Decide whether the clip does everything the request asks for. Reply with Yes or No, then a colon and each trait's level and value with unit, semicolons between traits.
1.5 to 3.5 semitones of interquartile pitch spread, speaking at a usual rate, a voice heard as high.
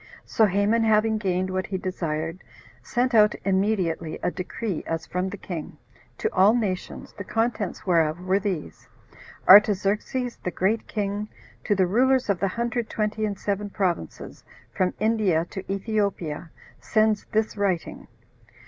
Yes: average, 2.9 semitones; average, 145 wpm; high, 200 Hz